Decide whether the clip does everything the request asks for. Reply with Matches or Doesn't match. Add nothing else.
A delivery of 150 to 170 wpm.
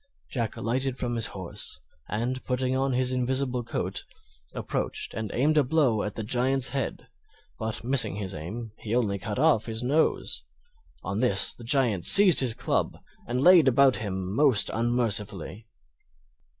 Matches